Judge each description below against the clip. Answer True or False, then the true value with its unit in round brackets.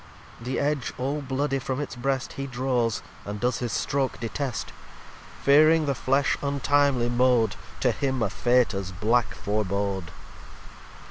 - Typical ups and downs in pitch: True (3.3 semitones)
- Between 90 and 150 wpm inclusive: True (140 wpm)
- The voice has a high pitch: False (125 Hz)